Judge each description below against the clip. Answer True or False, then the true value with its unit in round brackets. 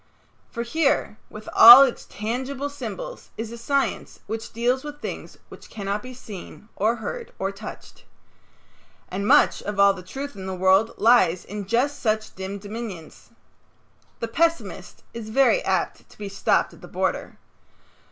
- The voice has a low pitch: False (225 Hz)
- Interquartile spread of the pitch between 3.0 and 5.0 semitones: True (4.7 semitones)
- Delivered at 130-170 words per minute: True (160 wpm)